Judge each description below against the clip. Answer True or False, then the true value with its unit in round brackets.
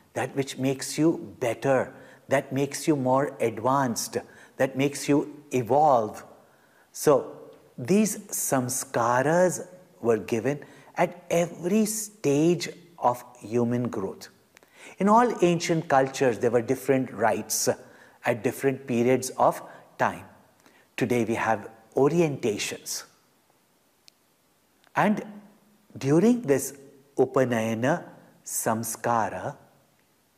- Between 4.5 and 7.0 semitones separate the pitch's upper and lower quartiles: True (5.4 semitones)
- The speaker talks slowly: True (95 wpm)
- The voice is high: False (135 Hz)